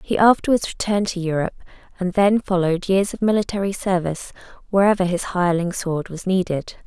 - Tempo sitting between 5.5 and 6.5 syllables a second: Yes, 6.4 syllables/s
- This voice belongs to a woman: Yes, female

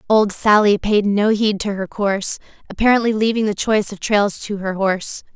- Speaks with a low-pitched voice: No, high, 205 Hz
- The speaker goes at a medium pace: Yes, average, 190 wpm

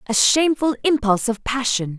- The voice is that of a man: No, female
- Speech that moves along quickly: No, average, 150 wpm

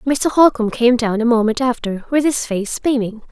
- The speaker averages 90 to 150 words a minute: No, average, 200 wpm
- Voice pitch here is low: No, high, 240 Hz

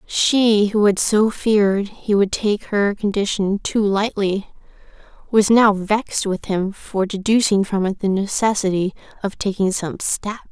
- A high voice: Yes, high, 205 Hz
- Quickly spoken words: No, average, 155 wpm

